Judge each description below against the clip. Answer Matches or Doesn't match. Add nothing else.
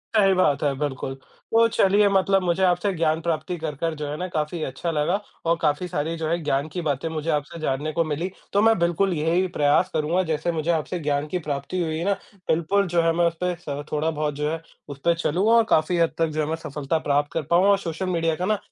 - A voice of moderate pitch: Matches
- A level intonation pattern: Doesn't match